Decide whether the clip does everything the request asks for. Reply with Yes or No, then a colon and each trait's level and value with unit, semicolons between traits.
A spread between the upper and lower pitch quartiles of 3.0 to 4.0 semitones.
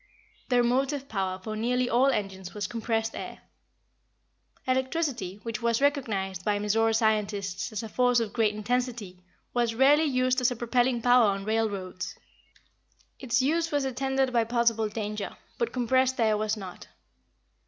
Yes: average, 3.3 semitones